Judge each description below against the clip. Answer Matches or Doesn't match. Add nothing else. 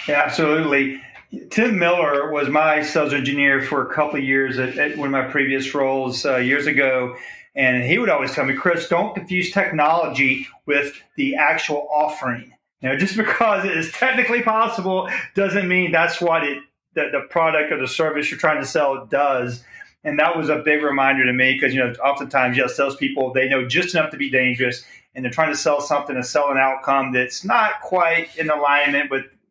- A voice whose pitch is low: Doesn't match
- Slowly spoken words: Doesn't match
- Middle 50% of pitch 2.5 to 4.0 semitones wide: Matches